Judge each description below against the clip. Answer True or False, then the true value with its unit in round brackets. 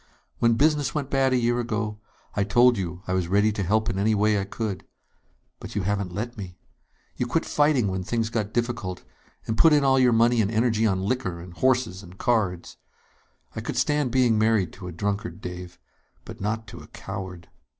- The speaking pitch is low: True (110 Hz)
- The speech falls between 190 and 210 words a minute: True (200 wpm)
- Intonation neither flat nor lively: True (4.2 semitones)